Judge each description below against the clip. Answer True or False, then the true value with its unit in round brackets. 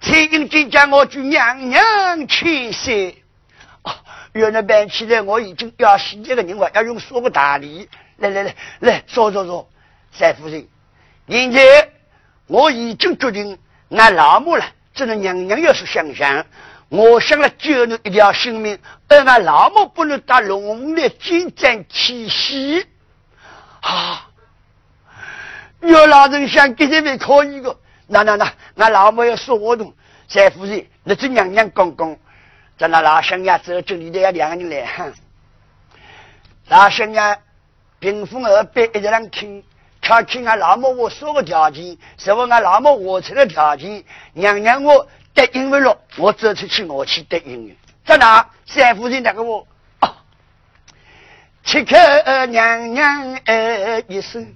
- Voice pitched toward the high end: True (225 Hz)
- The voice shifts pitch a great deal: True (5.9 semitones)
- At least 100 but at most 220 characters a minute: True (185 characters per minute)